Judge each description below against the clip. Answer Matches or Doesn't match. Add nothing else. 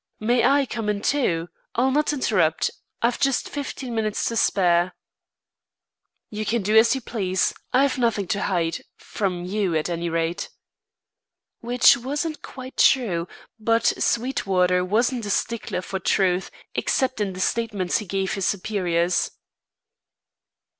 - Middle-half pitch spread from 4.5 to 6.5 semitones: Matches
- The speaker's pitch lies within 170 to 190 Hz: Doesn't match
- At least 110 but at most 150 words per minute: Matches